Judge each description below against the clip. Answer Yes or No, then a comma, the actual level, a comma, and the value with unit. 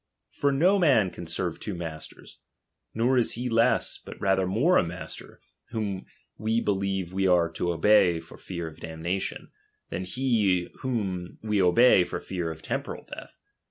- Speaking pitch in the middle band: No, very low, 95 Hz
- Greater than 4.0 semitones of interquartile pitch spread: Yes, average, 4.7 semitones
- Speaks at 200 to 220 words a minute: No, average, 160 wpm